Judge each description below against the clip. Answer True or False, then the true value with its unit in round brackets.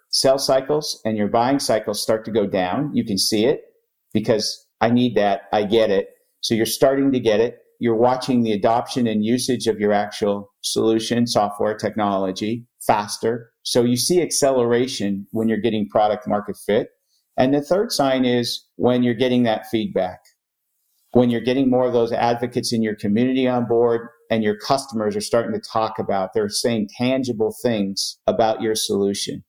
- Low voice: True (120 Hz)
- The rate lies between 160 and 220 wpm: True (175 wpm)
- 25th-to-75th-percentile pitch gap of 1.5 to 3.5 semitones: True (2.7 semitones)